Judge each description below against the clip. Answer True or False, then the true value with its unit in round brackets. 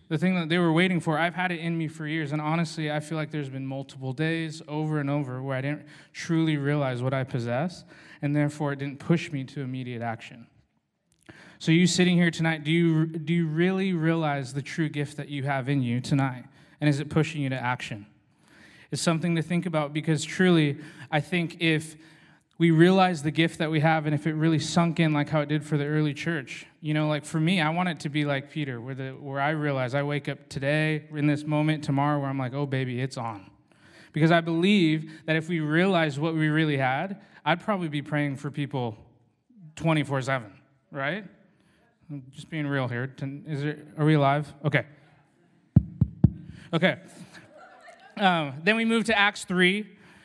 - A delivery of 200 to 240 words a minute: True (205 wpm)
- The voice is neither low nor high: True (150 Hz)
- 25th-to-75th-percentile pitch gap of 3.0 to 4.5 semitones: False (2.6 semitones)